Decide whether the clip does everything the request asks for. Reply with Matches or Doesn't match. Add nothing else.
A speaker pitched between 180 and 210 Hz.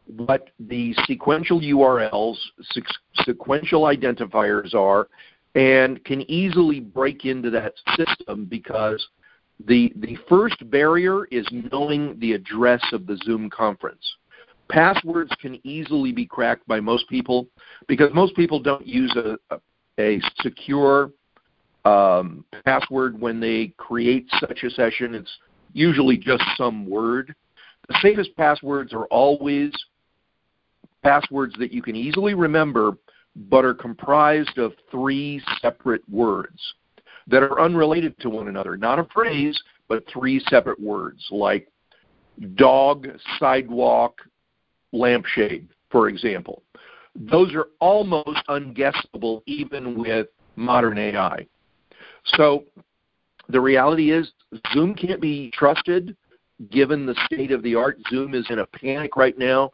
Doesn't match